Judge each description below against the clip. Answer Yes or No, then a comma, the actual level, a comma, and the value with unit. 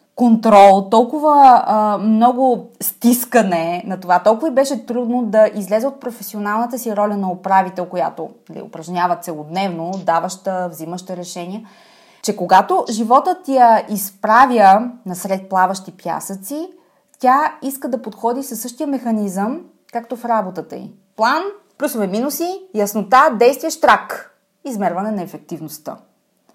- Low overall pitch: No, high, 215 Hz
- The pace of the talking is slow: No, average, 125 wpm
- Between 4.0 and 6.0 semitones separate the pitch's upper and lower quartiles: Yes, average, 5.2 semitones